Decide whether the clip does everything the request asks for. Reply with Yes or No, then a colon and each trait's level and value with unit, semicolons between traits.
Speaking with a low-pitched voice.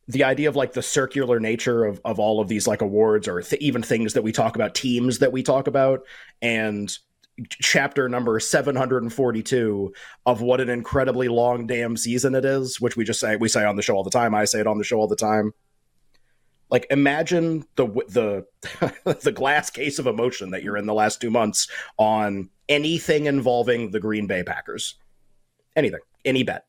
Yes: low, 120 Hz